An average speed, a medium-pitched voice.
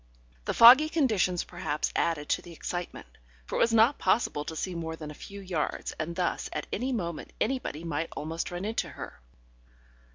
Yes: average, 185 wpm; medium, 175 Hz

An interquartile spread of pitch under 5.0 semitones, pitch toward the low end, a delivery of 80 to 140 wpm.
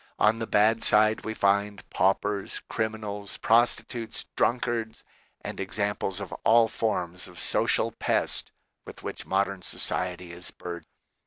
Yes: narrow, 2.5 semitones; low, 105 Hz; slow, 135 wpm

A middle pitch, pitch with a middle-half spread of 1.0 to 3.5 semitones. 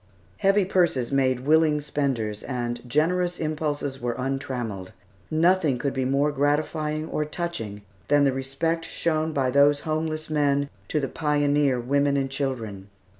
Yes: medium, 145 Hz; average, 3.0 semitones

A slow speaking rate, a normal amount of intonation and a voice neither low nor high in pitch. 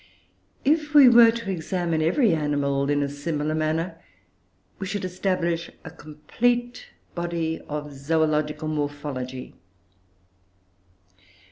Yes: slow, 105 wpm; average, 4.1 semitones; medium, 160 Hz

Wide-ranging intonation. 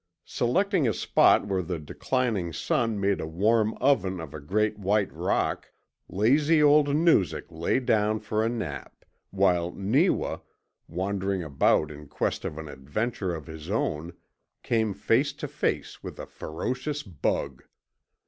Yes: wide, 6.3 semitones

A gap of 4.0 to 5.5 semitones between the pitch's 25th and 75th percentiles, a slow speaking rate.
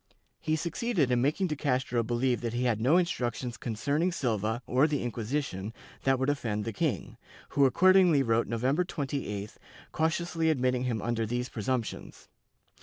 No: average, 4.5 semitones; average, 160 wpm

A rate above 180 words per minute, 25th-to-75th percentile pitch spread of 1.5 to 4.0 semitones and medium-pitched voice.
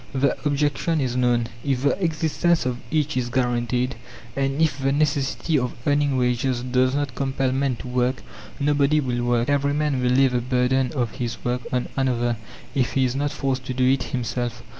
No: average, 190 wpm; narrow, 2.4 semitones; low, 130 Hz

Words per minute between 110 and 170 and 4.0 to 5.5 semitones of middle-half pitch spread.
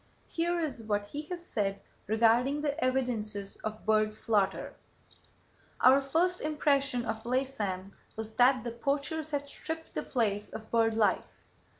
Yes: average, 140 wpm; average, 4.9 semitones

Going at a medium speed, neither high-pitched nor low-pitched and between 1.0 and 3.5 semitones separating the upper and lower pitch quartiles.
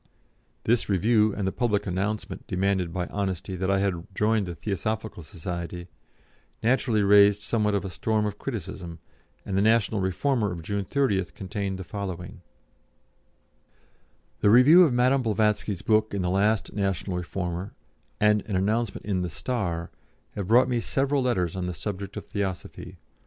No: average, 155 wpm; low, 100 Hz; average, 2.9 semitones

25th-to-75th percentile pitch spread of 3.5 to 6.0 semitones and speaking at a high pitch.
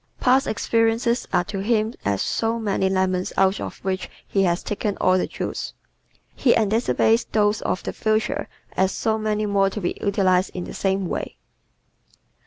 No: average, 2.8 semitones; high, 205 Hz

